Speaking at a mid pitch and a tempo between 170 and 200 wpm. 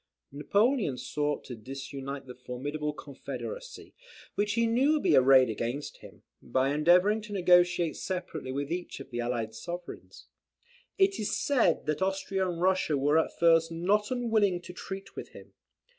No: medium, 170 Hz; average, 160 wpm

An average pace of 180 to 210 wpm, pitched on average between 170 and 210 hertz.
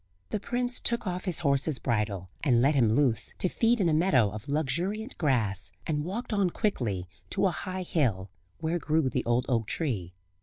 No: average, 190 wpm; medium, 150 Hz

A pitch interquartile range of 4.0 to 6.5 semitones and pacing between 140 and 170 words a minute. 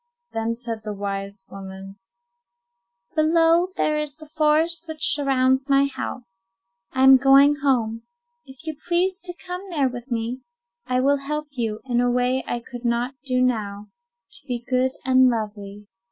Yes: average, 4.4 semitones; average, 160 wpm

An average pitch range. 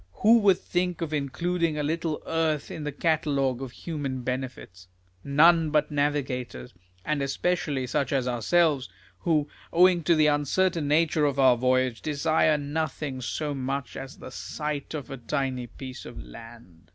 Yes: average, 3.6 semitones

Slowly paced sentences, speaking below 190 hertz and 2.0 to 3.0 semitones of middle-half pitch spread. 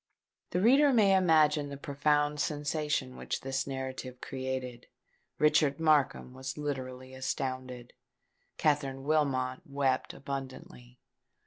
Yes: slow, 105 wpm; medium, 140 Hz; narrow, 2.4 semitones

